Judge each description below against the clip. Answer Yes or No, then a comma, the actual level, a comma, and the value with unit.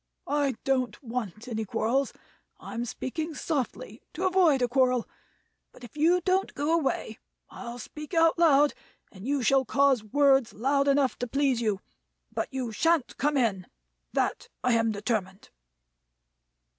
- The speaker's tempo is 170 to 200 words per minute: No, average, 145 wpm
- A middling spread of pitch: Yes, average, 4.0 semitones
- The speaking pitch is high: Yes, very high, 265 Hz